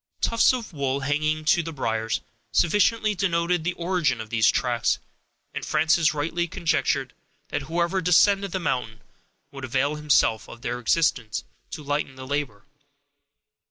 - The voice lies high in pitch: No, medium, 155 Hz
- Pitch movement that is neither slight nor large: Yes, average, 4.8 semitones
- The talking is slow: No, average, 145 wpm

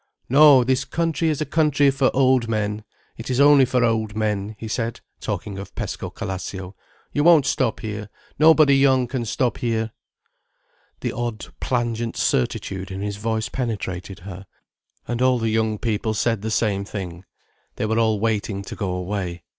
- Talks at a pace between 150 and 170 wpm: Yes, average, 165 wpm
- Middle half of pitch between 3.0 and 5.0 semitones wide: Yes, average, 4.0 semitones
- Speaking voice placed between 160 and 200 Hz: No, low, 115 Hz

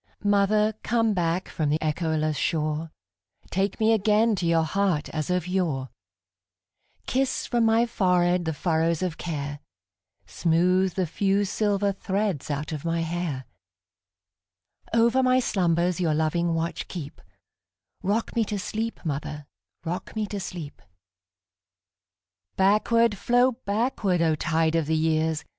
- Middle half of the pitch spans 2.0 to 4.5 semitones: No, wide, 5.4 semitones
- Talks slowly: Yes, slow, 115 wpm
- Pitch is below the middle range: No, medium, 170 Hz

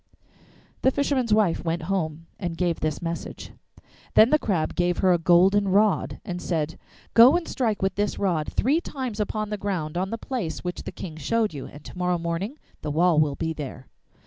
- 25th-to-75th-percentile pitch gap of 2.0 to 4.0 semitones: No, average, 4.6 semitones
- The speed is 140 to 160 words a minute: No, average, 200 wpm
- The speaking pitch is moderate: Yes, medium, 180 Hz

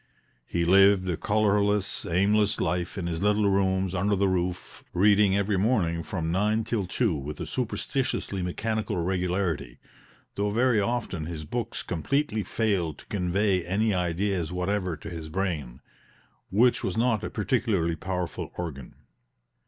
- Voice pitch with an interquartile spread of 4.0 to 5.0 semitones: No, average, 3.2 semitones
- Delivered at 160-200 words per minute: No, average, 145 wpm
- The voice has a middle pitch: No, very low, 95 Hz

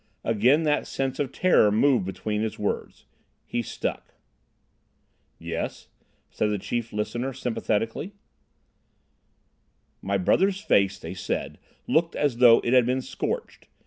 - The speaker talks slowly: Yes, slow, 125 wpm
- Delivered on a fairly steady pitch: No, average, 4.4 semitones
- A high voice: No, low, 120 Hz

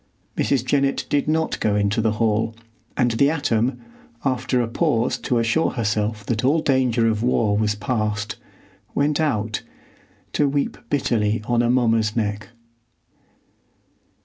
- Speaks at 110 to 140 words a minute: Yes, slow, 135 wpm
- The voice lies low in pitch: Yes, low, 115 Hz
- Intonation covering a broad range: No, average, 3.6 semitones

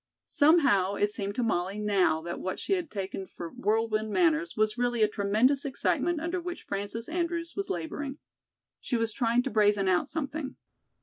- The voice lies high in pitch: Yes, high, 225 Hz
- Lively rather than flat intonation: Yes, wide, 7.1 semitones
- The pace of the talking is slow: No, average, 175 wpm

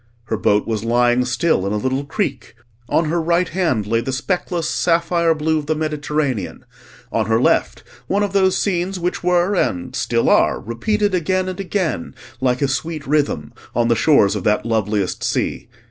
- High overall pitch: No, medium, 150 Hz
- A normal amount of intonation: No, wide, 7.2 semitones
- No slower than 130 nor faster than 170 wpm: No, average, 180 wpm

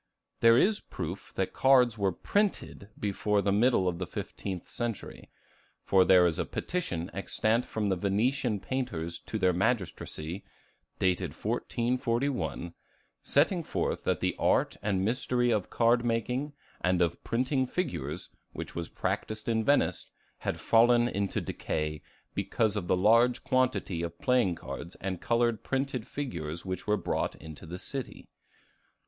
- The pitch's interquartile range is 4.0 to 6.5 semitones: Yes, average, 5.2 semitones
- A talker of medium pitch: No, low, 110 Hz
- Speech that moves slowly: No, average, 145 wpm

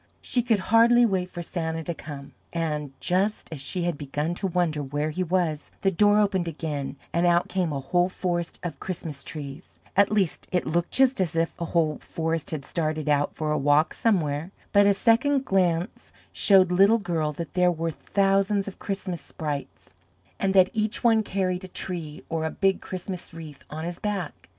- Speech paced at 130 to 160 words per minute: No, average, 190 wpm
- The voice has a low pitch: No, medium, 175 Hz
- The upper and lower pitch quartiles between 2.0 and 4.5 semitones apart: Yes, average, 3.7 semitones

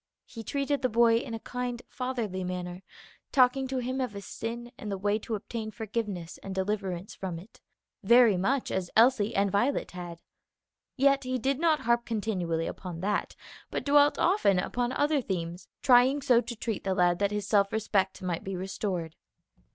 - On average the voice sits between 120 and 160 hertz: No, high, 215 Hz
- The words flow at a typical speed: Yes, average, 180 wpm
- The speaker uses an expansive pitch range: No, average, 4.8 semitones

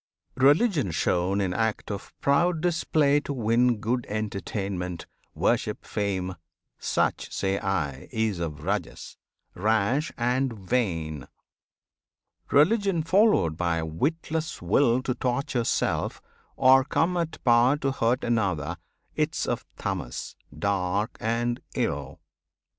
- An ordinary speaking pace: No, slow, 115 wpm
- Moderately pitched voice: No, low, 115 Hz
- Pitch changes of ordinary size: No, wide, 6.7 semitones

